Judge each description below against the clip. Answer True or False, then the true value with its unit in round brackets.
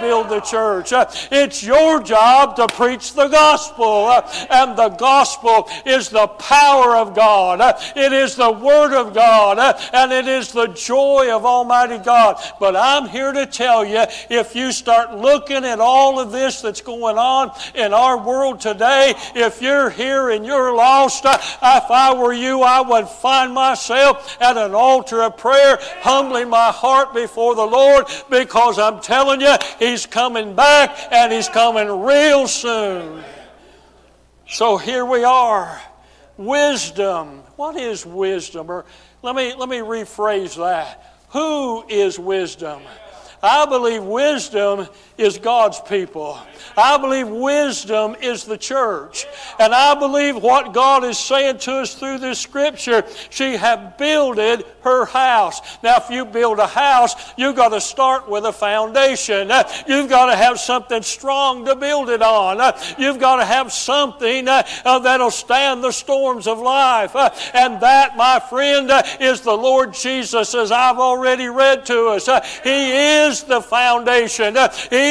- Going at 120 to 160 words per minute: True (155 wpm)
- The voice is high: True (250 Hz)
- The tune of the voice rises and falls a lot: False (3.1 semitones)